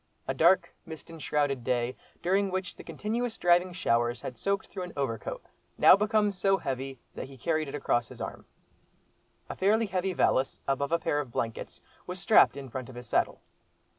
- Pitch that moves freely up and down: Yes, wide, 6.4 semitones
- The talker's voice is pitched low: No, medium, 160 Hz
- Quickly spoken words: No, average, 185 wpm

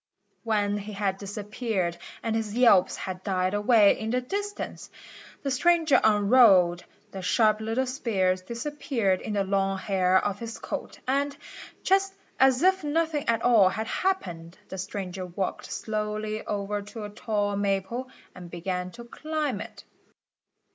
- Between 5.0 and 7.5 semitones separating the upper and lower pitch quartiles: No, average, 4.5 semitones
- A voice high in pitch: Yes, high, 210 Hz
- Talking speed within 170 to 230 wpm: No, average, 150 wpm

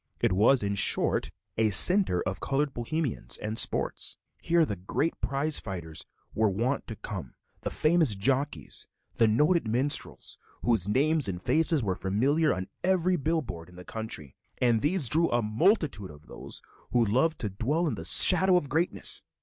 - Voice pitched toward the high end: No, low, 125 Hz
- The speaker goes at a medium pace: Yes, average, 170 wpm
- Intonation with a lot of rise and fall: Yes, wide, 7.6 semitones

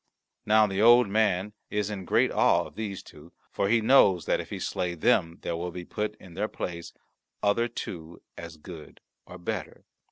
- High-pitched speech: No, very low, 95 Hz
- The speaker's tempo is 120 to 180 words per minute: No, average, 190 wpm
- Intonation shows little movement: No, average, 3.7 semitones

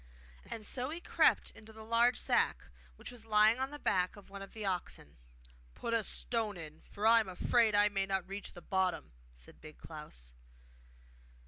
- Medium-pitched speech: No, high, 205 Hz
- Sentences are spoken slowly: No, average, 190 wpm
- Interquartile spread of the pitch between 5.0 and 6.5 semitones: No, average, 3.5 semitones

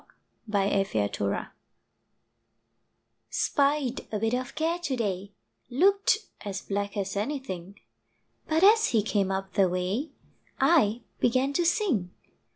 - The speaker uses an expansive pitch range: Yes, wide, 7.1 semitones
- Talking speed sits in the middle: No, slow, 115 wpm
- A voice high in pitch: Yes, high, 225 Hz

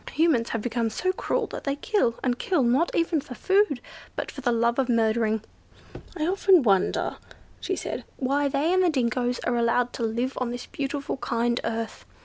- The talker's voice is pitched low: No, very high, 250 Hz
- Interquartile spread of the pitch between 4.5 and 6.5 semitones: No, average, 4.1 semitones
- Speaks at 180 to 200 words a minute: Yes, average, 190 wpm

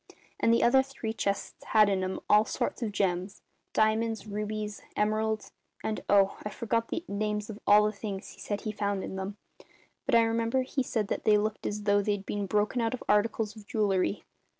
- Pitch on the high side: Yes, high, 210 Hz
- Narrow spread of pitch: Yes, narrow, 1.6 semitones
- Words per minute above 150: Yes, average, 200 wpm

